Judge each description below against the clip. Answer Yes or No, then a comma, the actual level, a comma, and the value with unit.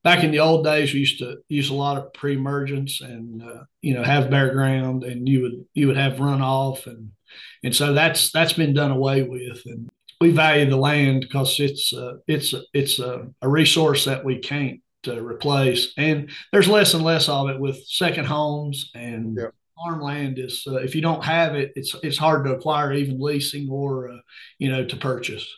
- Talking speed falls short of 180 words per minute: No, average, 200 wpm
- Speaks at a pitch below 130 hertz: No, medium, 140 Hz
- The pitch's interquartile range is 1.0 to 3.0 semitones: Yes, narrow, 2.4 semitones